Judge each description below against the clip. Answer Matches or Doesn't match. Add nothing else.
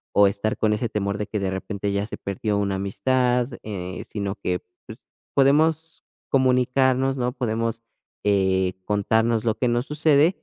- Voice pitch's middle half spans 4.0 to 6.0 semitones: Matches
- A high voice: Doesn't match